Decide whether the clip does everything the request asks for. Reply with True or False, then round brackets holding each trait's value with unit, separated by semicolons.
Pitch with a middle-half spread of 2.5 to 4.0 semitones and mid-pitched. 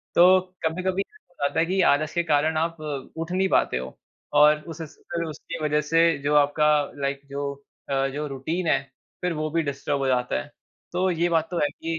True (2.9 semitones; 155 Hz)